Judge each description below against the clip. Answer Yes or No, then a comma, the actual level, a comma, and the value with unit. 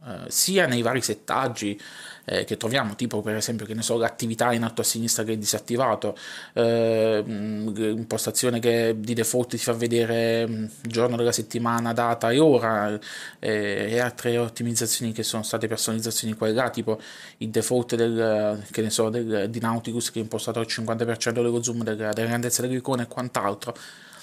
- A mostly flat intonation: Yes, narrow, 1.2 semitones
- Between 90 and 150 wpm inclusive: No, fast, 170 wpm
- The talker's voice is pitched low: Yes, low, 115 Hz